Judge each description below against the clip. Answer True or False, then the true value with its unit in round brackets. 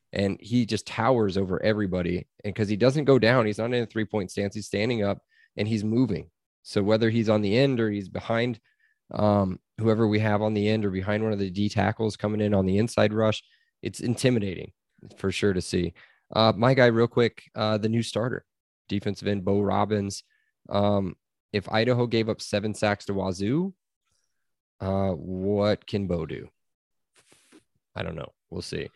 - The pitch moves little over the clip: True (2.0 semitones)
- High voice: False (105 Hz)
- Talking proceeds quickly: False (190 wpm)